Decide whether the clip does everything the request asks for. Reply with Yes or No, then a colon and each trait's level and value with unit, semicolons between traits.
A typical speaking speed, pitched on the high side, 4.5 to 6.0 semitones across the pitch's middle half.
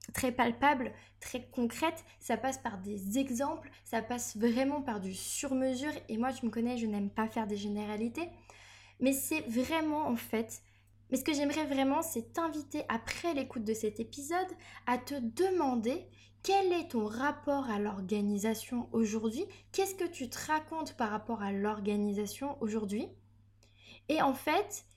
Yes: average, 160 wpm; high, 245 Hz; average, 5.3 semitones